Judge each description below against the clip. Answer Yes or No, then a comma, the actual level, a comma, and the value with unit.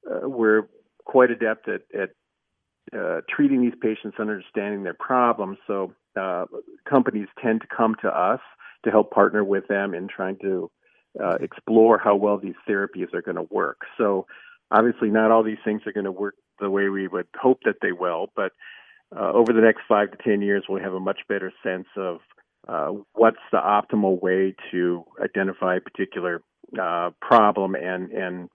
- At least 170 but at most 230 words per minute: Yes, average, 185 wpm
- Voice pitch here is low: Yes, low, 105 Hz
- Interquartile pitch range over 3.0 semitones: No, narrow, 2.5 semitones